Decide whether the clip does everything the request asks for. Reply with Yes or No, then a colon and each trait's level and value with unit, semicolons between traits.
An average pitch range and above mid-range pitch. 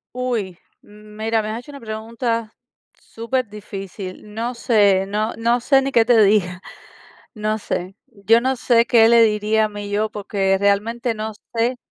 No: narrow, 2.1 semitones; high, 220 Hz